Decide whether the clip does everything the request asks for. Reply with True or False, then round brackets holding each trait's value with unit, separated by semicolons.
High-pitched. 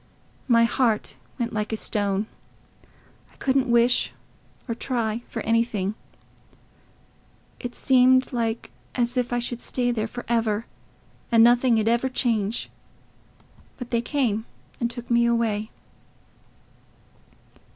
True (235 Hz)